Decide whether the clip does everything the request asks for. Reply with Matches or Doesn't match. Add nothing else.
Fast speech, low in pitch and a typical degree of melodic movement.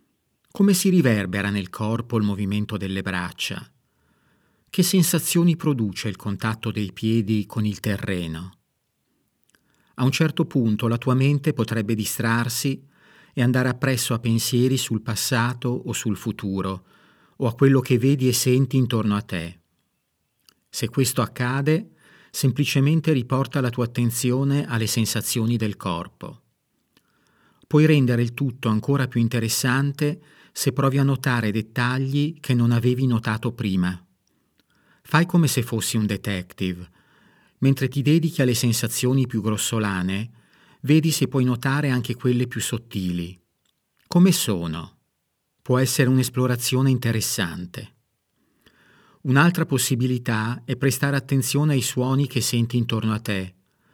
Doesn't match